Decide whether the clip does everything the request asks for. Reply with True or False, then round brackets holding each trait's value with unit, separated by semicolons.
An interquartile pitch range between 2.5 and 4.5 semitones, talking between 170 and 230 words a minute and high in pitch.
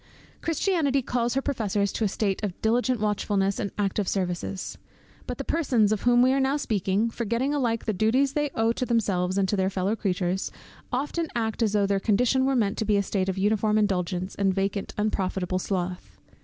True (3.9 semitones; 195 wpm; 210 Hz)